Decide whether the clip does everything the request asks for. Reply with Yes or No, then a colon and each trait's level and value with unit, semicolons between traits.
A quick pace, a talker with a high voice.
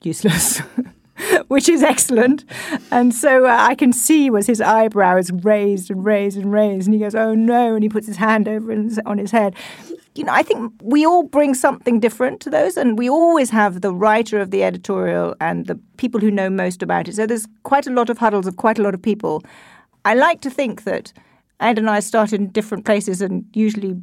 Yes: fast, 220 wpm; high, 220 Hz